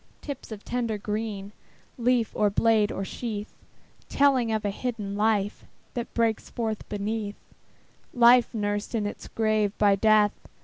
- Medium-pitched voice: No, high, 215 Hz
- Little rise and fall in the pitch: Yes, narrow, 2.1 semitones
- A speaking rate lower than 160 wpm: Yes, average, 140 wpm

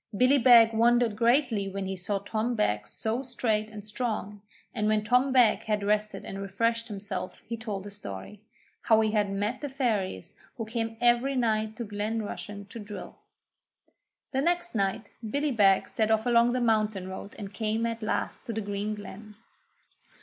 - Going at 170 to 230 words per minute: Yes, average, 180 wpm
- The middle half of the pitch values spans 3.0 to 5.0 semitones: No, narrow, 2.4 semitones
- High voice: Yes, high, 215 Hz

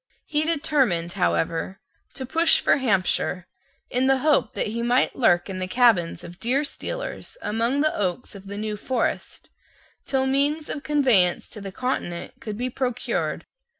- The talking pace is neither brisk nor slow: Yes, average, 155 wpm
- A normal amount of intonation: No, wide, 6.3 semitones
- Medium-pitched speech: No, high, 245 Hz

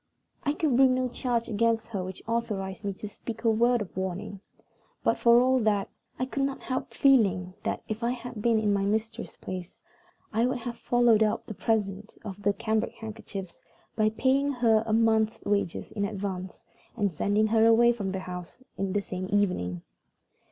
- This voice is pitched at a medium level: No, high, 220 Hz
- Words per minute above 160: Yes, average, 185 wpm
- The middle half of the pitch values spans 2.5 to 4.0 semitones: Yes, average, 3.1 semitones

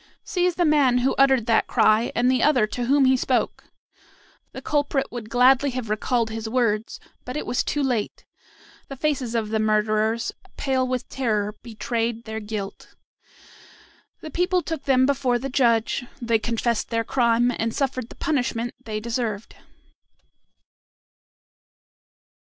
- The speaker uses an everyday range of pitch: Yes, average, 3.1 semitones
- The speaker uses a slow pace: No, average, 145 wpm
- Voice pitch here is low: No, high, 245 Hz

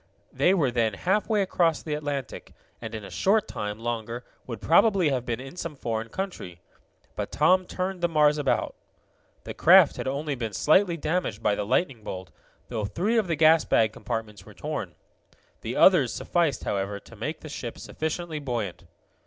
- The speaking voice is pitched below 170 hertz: Yes, medium, 140 Hz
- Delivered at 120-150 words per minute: No, average, 180 wpm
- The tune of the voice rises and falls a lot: Yes, wide, 7.3 semitones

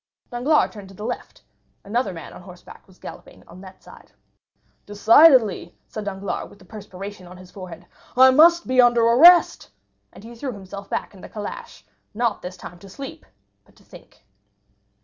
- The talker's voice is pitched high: Yes, high, 205 Hz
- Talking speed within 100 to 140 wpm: No, average, 175 wpm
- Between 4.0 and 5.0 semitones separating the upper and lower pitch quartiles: Yes, average, 4.7 semitones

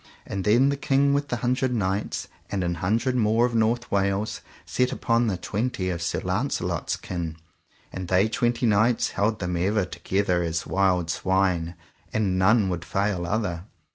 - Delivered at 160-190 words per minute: Yes, average, 170 wpm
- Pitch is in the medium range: No, low, 100 Hz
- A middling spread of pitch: Yes, average, 4.4 semitones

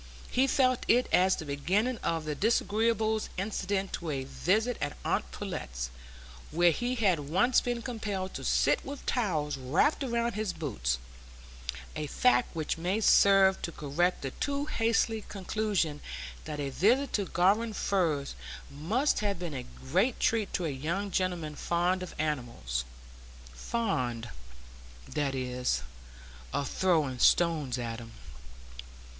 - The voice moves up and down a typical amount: No, wide, 7.5 semitones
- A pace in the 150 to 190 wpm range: No, average, 140 wpm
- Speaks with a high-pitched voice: No, medium, 175 Hz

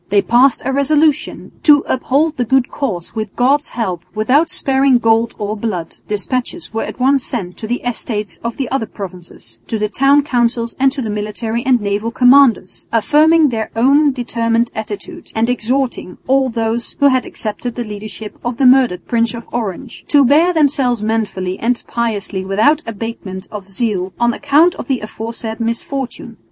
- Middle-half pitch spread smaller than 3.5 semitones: No, average, 3.9 semitones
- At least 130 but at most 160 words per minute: No, average, 170 wpm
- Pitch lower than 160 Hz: No, high, 235 Hz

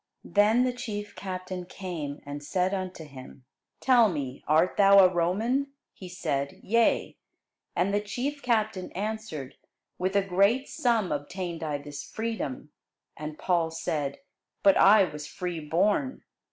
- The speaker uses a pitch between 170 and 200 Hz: Yes, medium, 185 Hz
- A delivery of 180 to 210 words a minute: No, average, 140 wpm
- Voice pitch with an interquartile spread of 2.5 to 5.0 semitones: No, wide, 5.6 semitones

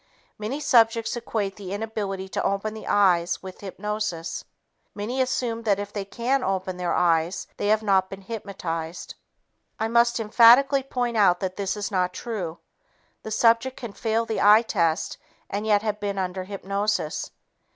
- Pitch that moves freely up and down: No, average, 3.1 semitones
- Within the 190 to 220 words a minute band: No, average, 160 wpm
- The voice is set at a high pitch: Yes, high, 205 Hz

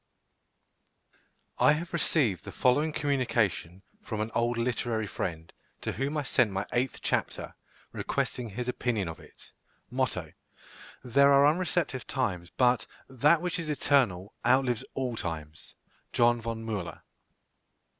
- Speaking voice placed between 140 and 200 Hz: No, low, 120 Hz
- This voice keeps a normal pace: No, slow, 130 wpm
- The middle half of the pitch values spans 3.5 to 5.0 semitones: Yes, average, 4.6 semitones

